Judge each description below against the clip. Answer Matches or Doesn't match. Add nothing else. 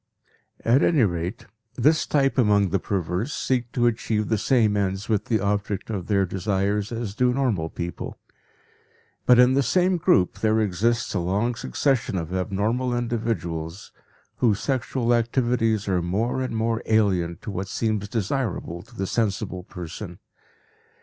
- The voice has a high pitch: Doesn't match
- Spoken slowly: Doesn't match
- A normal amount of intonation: Matches